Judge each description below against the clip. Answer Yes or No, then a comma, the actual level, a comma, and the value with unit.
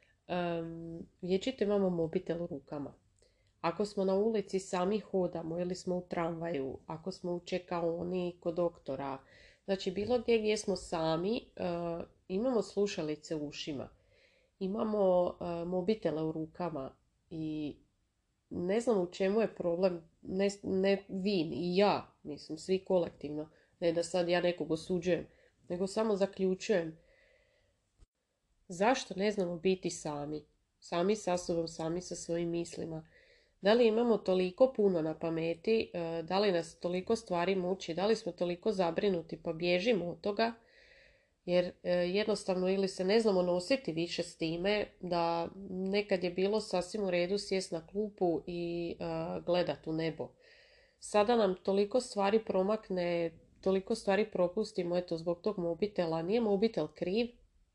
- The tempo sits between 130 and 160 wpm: Yes, average, 140 wpm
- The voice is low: No, medium, 180 Hz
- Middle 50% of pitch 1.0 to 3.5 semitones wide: Yes, average, 3.1 semitones